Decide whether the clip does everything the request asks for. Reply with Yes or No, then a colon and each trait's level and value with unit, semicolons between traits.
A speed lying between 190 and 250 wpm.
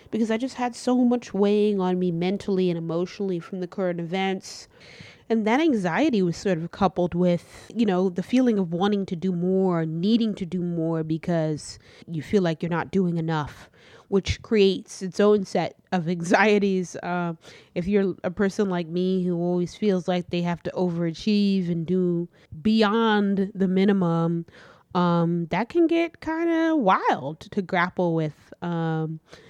No: average, 170 wpm